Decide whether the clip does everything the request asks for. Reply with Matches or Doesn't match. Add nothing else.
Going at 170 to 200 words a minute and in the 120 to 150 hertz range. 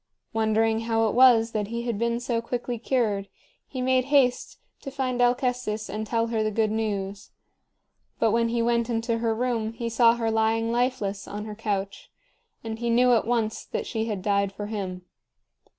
Doesn't match